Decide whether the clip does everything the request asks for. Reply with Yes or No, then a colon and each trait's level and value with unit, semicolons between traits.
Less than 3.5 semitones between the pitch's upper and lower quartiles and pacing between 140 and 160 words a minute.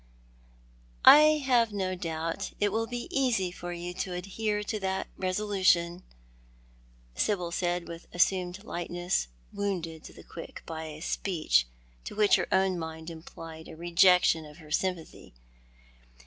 Yes: average, 3.1 semitones; average, 150 wpm